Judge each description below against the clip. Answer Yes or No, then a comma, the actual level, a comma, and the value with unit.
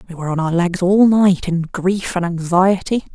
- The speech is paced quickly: Yes, fast, 210 wpm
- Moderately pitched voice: Yes, medium, 180 Hz